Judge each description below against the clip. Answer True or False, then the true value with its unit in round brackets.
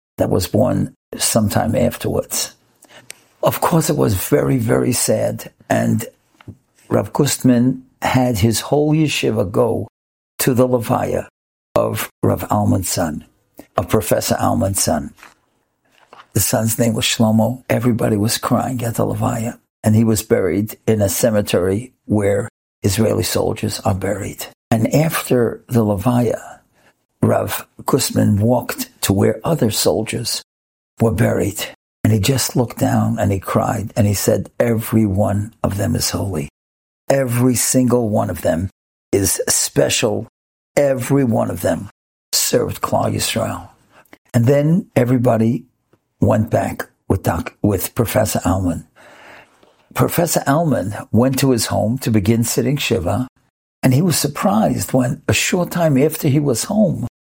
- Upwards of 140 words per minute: False (135 wpm)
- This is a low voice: True (115 Hz)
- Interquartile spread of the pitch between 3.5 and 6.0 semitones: False (3.1 semitones)